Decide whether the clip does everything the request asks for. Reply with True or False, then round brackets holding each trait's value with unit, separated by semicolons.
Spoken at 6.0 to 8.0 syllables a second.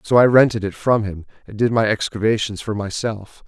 False (5.4 syllables/s)